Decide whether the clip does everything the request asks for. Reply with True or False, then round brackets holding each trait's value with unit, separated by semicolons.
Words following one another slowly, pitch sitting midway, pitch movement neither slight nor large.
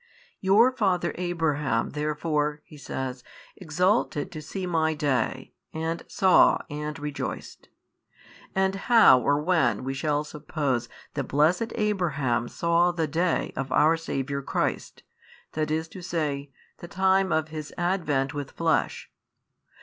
True (125 wpm; 155 Hz; 3.5 semitones)